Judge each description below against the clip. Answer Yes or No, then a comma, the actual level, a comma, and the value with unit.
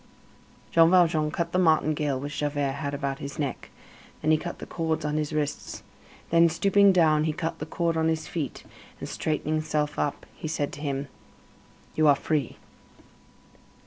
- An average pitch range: No, narrow, 2.0 semitones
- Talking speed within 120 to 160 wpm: No, average, 175 wpm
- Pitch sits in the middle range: Yes, medium, 155 Hz